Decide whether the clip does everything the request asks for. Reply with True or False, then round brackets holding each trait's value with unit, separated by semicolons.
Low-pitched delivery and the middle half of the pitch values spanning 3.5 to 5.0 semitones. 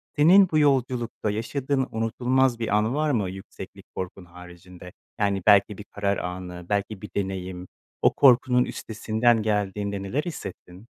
True (105 Hz; 4.7 semitones)